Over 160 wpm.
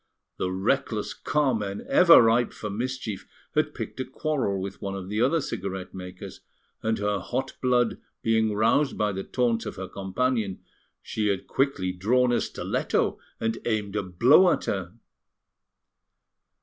No: average, 150 wpm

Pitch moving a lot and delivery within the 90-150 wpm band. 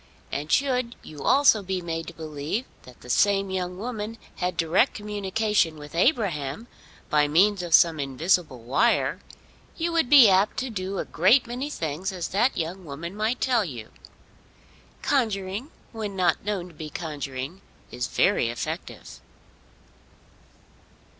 Yes: wide, 5.7 semitones; average, 145 wpm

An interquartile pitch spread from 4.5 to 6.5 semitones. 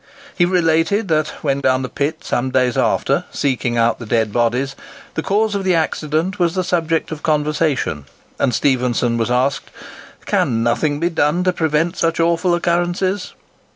Yes: average, 5.2 semitones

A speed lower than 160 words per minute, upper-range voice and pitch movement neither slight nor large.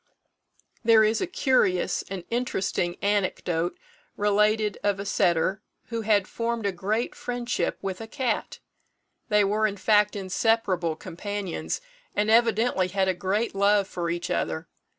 Yes: average, 140 wpm; high, 205 Hz; average, 3.0 semitones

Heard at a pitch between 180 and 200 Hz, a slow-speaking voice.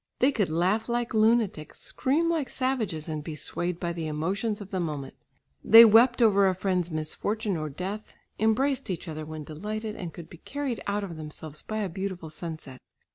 No: high, 190 Hz; average, 185 wpm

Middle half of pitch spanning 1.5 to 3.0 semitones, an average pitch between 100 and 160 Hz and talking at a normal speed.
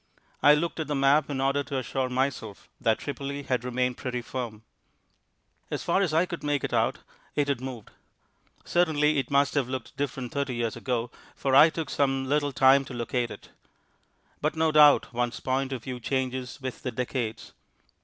Yes: narrow, 2.4 semitones; low, 135 Hz; average, 185 wpm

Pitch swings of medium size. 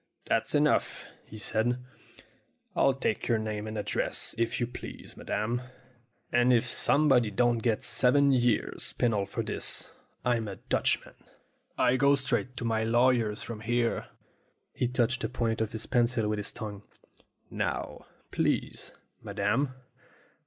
No: narrow, 2.3 semitones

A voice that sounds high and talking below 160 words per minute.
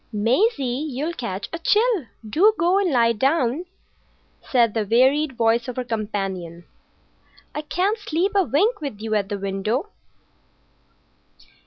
Yes: very high, 255 Hz; average, 140 wpm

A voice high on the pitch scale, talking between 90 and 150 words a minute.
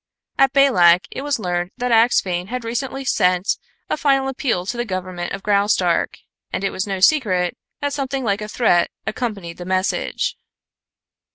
No: high, 210 Hz; average, 165 wpm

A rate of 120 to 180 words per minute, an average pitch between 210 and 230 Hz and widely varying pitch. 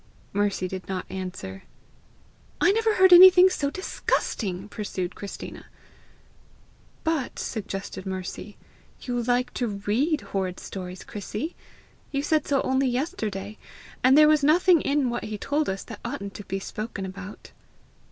Yes: average, 140 wpm; high, 225 Hz; wide, 7.1 semitones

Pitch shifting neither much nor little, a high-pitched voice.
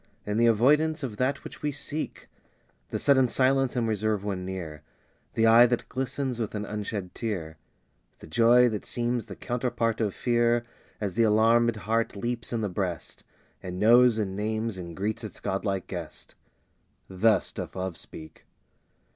No: average, 3.5 semitones; low, 110 Hz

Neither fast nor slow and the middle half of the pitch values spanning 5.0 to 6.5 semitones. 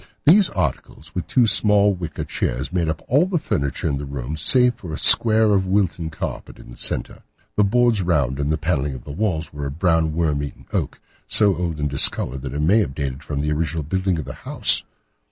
No: fast, 225 wpm; wide, 5.6 semitones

